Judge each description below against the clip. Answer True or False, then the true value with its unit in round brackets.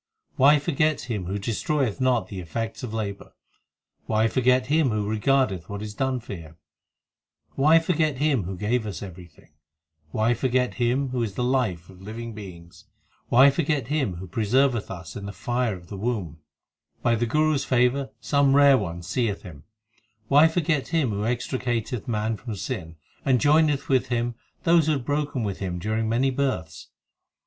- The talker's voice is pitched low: True (120 Hz)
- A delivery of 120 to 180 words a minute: True (175 wpm)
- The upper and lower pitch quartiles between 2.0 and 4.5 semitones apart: False (5.0 semitones)